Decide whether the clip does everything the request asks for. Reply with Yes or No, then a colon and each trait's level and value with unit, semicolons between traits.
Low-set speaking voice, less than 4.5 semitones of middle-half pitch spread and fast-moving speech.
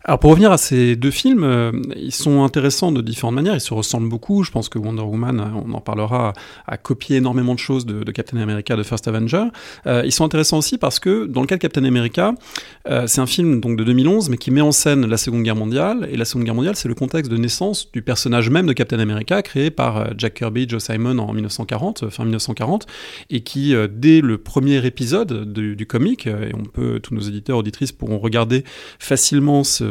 Yes: low, 125 Hz; average, 4.1 semitones; fast, 230 wpm